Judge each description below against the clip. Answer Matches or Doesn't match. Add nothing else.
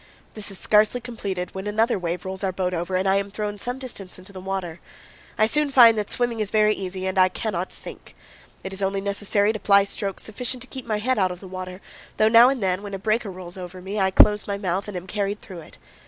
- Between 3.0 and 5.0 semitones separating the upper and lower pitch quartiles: Doesn't match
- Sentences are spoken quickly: Matches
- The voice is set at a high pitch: Matches